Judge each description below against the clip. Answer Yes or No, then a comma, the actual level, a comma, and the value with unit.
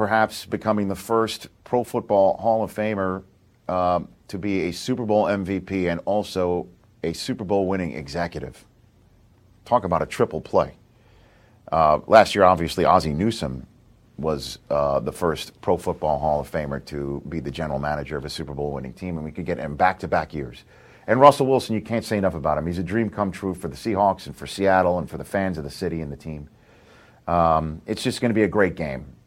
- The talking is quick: Yes, fast, 210 wpm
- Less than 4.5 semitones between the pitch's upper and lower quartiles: No, average, 5.2 semitones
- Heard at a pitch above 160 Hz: No, very low, 95 Hz